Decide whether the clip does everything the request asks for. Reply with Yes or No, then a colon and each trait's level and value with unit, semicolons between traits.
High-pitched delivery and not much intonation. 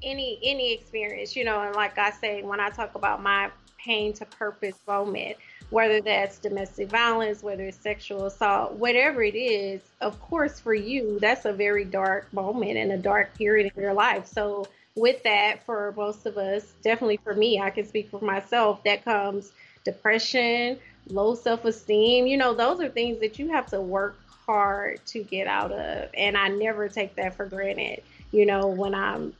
Yes: high, 210 Hz; narrow, 2.0 semitones